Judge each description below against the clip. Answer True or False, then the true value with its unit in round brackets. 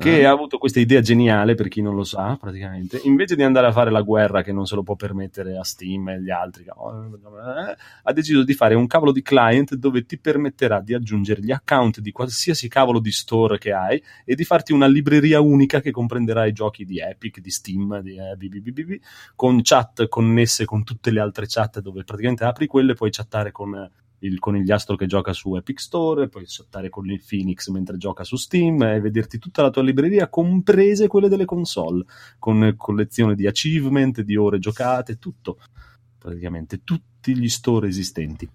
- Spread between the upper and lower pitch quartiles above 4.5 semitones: True (5.0 semitones)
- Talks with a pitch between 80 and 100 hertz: False (115 Hz)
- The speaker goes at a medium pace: False (200 wpm)